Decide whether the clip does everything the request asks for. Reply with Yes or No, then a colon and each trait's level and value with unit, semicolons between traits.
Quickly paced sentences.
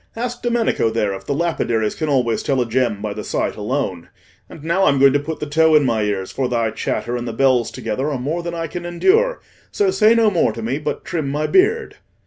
Yes: fast, 240 wpm